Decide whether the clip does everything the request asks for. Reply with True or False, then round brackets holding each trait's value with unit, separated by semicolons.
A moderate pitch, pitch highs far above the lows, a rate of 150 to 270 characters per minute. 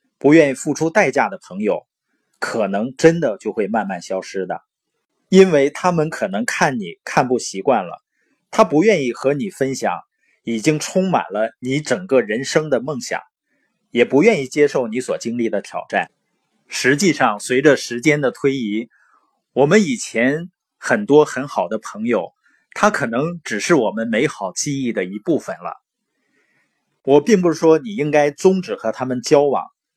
True (150 Hz; 6.0 semitones; 240 characters per minute)